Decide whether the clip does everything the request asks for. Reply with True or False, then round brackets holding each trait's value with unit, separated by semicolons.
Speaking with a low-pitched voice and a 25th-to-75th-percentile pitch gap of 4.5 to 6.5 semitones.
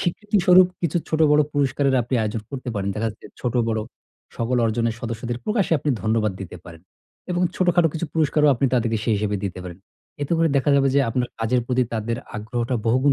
True (125 Hz; 5.2 semitones)